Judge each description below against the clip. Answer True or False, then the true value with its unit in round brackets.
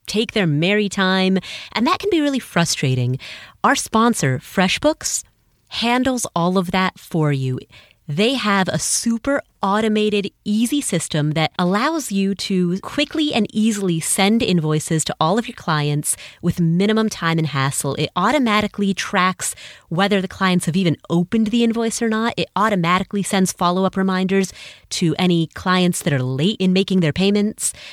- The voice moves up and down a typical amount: True (4.5 semitones)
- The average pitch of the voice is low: False (190 Hz)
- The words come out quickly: False (160 wpm)